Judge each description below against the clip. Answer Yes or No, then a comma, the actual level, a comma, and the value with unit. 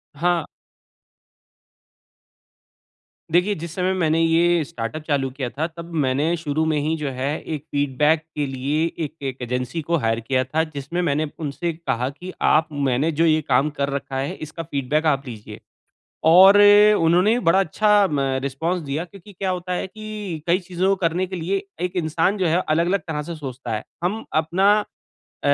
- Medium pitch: Yes, medium, 160 Hz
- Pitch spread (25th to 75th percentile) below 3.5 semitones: No, average, 4.0 semitones